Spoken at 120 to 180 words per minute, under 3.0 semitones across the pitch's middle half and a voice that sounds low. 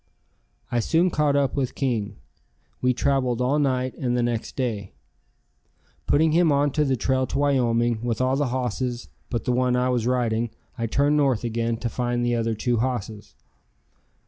Yes: average, 170 wpm; narrow, 2.5 semitones; low, 125 Hz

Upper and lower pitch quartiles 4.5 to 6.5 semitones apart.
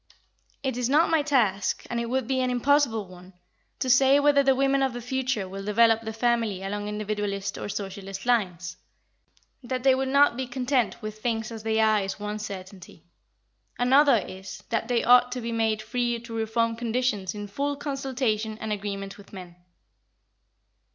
No: average, 3.8 semitones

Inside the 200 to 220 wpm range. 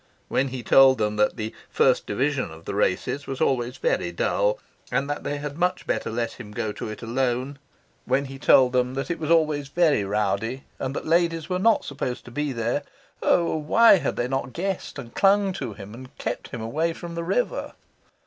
Yes: fast, 205 wpm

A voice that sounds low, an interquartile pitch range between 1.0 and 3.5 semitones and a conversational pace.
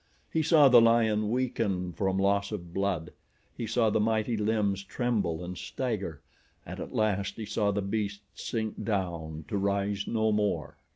Yes: low, 105 Hz; narrow, 2.4 semitones; average, 165 wpm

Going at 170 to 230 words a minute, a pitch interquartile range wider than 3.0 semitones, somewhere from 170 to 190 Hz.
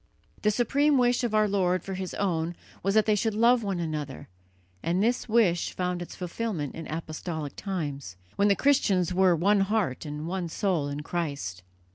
Yes: average, 180 wpm; average, 4.7 semitones; medium, 185 Hz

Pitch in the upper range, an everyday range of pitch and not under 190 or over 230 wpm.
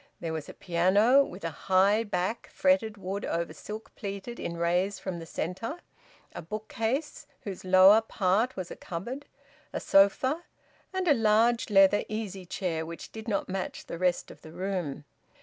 No: high, 195 Hz; average, 3.8 semitones; average, 165 wpm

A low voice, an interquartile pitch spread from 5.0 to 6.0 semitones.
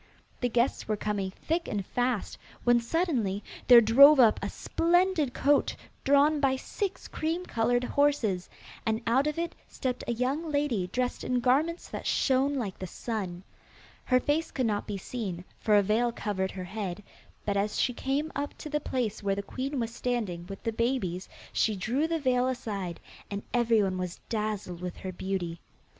No: high, 235 Hz; wide, 5.5 semitones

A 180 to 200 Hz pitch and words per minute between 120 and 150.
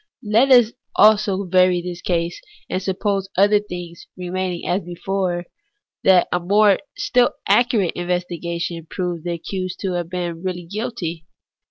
Yes: medium, 185 Hz; average, 145 wpm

